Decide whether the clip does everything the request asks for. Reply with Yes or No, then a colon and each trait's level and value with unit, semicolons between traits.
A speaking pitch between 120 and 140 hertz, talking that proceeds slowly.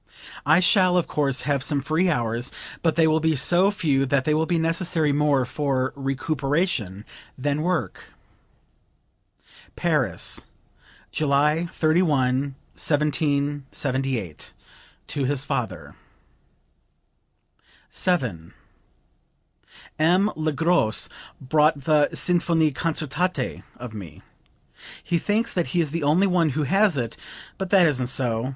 No: medium, 150 Hz; slow, 120 wpm